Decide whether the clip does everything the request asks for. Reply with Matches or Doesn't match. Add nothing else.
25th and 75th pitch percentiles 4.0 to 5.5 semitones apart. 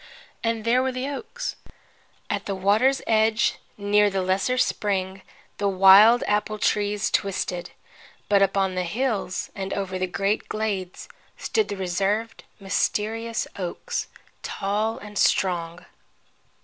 Doesn't match